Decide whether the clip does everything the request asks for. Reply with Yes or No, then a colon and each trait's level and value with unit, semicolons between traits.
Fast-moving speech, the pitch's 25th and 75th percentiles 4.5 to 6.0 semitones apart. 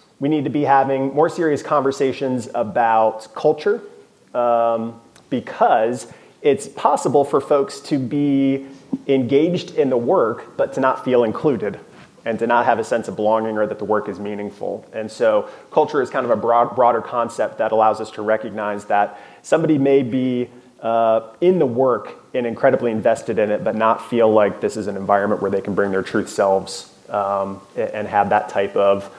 No: average, 185 wpm; average, 4.8 semitones